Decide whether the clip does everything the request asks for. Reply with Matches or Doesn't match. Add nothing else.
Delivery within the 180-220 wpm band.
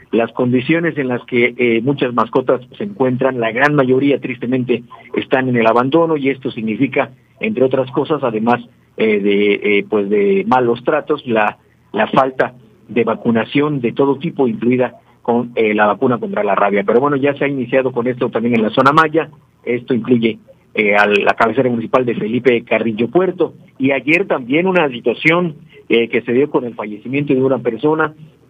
Matches